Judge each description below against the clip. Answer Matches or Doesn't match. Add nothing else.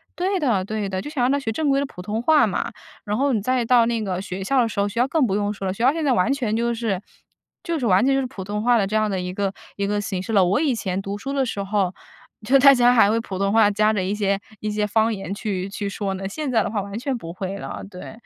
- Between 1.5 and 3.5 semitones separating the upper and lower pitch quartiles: Doesn't match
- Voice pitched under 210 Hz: Doesn't match